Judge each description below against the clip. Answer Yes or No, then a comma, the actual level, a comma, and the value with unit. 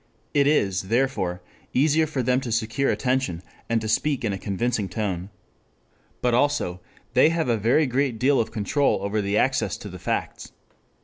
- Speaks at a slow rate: No, average, 175 wpm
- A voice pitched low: Yes, low, 120 Hz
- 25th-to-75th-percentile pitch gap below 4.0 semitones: No, average, 5.2 semitones